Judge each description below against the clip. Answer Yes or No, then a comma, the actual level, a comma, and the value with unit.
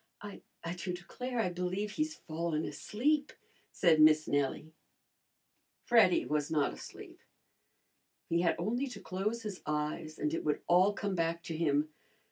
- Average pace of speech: Yes, average, 145 wpm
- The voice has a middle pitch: Yes, medium, 175 Hz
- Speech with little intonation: No, average, 5.1 semitones